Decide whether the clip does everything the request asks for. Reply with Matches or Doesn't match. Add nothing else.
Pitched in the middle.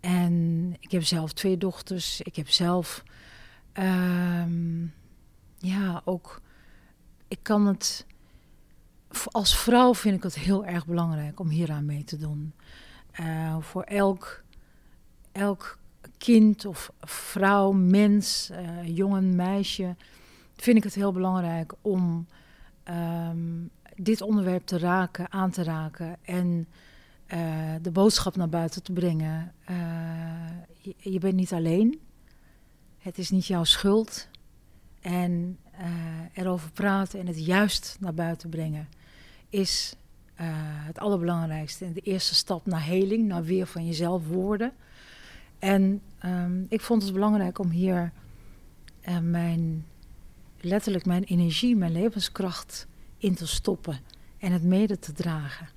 Matches